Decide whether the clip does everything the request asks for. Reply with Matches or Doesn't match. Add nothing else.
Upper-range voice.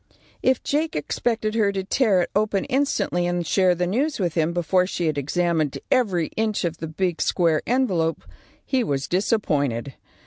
Doesn't match